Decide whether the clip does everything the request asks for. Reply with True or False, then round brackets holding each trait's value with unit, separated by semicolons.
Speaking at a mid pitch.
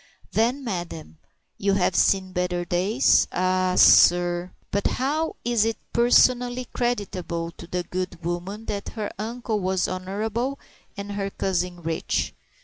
False (195 Hz)